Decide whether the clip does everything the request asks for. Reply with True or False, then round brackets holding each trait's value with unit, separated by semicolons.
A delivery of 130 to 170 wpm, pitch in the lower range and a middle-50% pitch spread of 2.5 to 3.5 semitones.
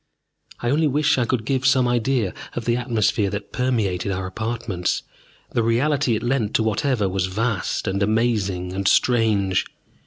False (160 wpm; 115 Hz; 4.0 semitones)